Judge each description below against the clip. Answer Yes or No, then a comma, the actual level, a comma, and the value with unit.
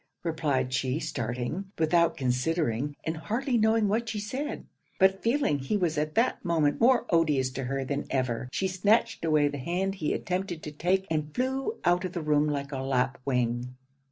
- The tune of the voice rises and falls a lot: Yes, wide, 6.1 semitones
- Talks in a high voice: No, medium, 160 Hz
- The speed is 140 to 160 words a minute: No, average, 180 wpm